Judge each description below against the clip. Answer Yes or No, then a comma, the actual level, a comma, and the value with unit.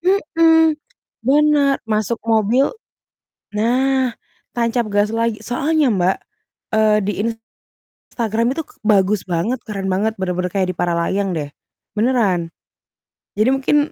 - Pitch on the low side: No, high, 225 Hz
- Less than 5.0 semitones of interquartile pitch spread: No, wide, 5.5 semitones